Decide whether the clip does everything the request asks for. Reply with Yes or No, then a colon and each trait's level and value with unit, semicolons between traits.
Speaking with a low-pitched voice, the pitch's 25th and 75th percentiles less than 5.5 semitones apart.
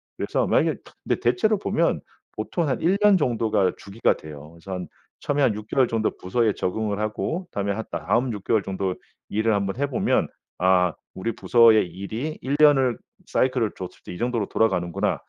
Yes: low, 110 Hz; average, 5.1 semitones